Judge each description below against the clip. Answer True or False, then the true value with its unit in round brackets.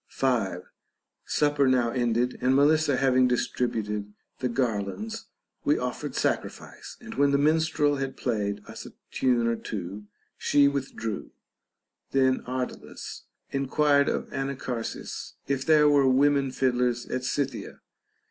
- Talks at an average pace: False (125 wpm)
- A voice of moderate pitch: False (130 Hz)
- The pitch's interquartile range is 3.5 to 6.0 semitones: False (3.1 semitones)